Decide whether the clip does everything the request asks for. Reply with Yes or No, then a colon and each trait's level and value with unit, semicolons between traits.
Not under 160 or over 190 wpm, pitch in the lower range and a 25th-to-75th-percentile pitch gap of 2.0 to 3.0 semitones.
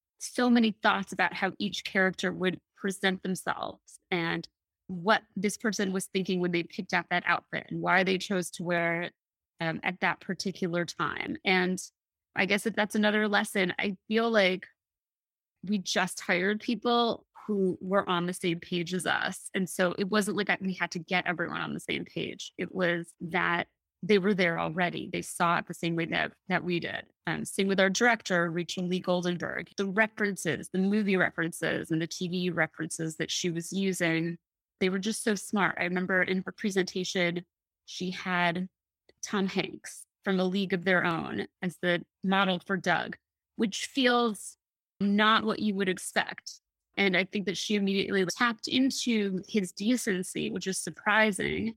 No: average, 175 wpm; medium, 185 Hz; average, 2.7 semitones